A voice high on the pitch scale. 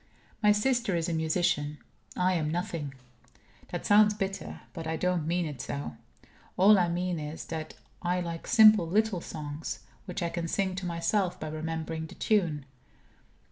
No: medium, 170 Hz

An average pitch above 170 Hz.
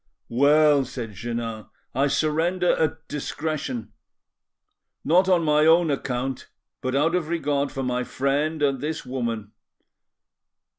No: medium, 140 Hz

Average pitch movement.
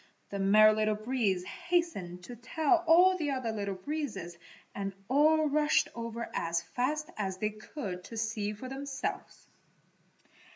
No: wide, 6.8 semitones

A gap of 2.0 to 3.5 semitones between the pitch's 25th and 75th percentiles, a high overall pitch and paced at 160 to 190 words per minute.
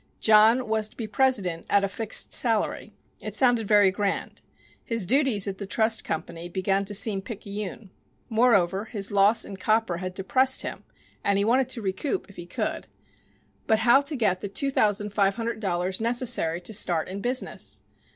Yes: average, 3.1 semitones; high, 210 Hz; average, 180 wpm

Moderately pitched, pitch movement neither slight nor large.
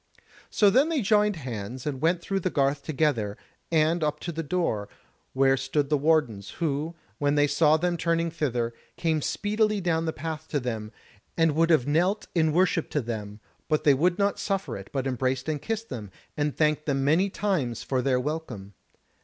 Yes: medium, 150 Hz; average, 4.3 semitones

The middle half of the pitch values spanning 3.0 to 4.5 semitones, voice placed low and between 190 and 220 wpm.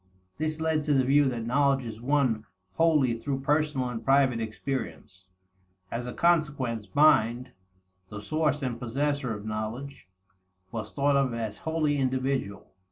No: average, 4.1 semitones; low, 130 Hz; average, 145 wpm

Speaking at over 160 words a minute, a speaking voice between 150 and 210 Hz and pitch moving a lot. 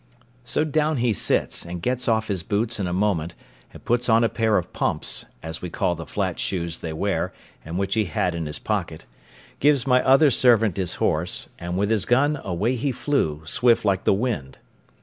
No: fast, 205 wpm; low, 105 Hz; wide, 6.0 semitones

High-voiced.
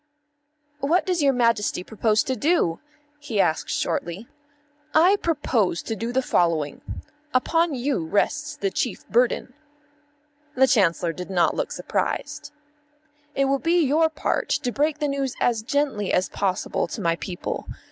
Yes: high, 245 Hz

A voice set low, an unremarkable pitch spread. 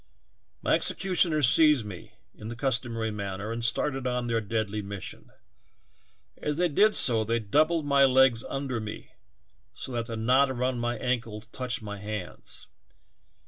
Yes: low, 120 Hz; average, 3.6 semitones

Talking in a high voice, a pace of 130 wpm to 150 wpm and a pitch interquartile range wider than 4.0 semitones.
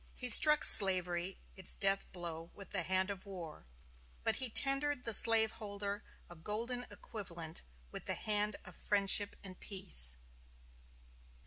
No: high, 200 Hz; slow, 135 wpm; average, 3.7 semitones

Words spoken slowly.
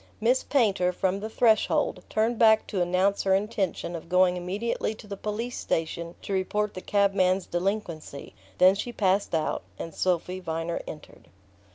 No: average, 160 wpm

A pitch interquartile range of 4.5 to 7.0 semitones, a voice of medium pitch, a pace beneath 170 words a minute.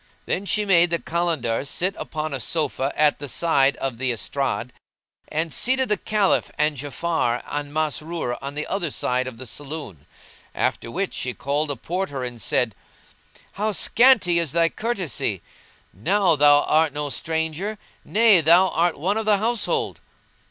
Yes: average, 5.1 semitones; medium, 155 Hz; average, 160 wpm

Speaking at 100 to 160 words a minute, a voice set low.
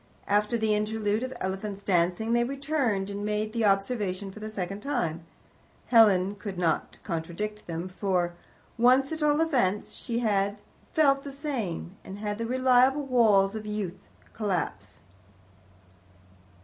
No: average, 145 wpm; high, 210 Hz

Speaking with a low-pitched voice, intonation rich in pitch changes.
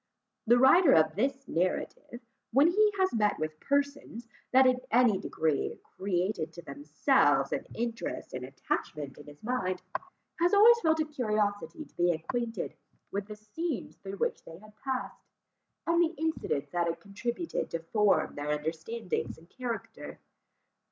No: high, 220 Hz; wide, 7.9 semitones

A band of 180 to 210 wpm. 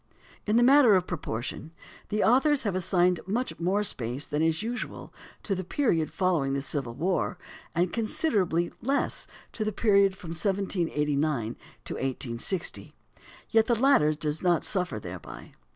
No: average, 150 wpm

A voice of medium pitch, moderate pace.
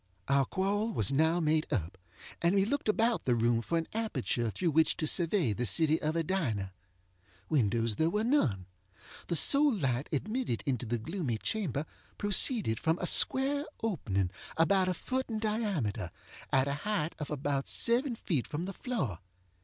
Yes: medium, 160 Hz; average, 170 wpm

